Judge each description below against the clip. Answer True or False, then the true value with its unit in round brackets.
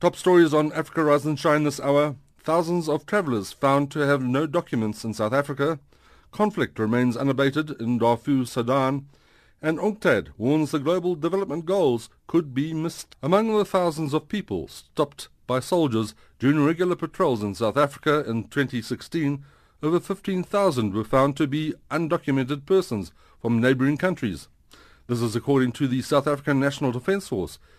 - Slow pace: False (155 wpm)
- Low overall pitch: False (145 Hz)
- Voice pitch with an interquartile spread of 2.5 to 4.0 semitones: False (4.5 semitones)